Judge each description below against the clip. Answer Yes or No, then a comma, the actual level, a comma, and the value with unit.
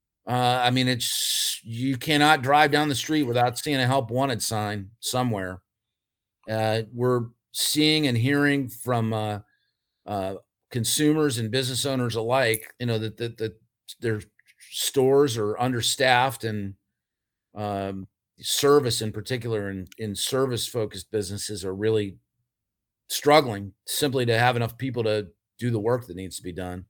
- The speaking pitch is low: Yes, low, 115 Hz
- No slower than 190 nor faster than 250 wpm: No, average, 150 wpm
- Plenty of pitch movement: No, average, 3.4 semitones